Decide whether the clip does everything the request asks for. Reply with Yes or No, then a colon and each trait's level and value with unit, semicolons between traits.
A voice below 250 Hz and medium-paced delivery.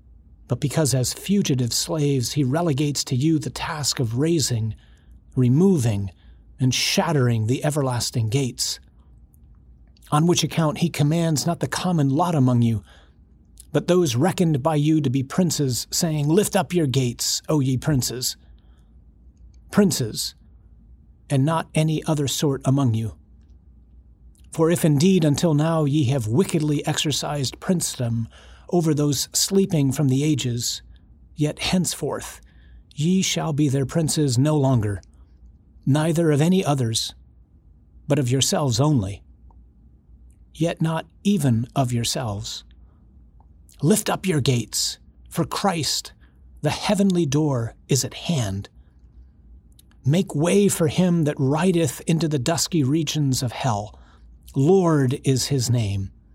No: low, 135 Hz; slow, 130 wpm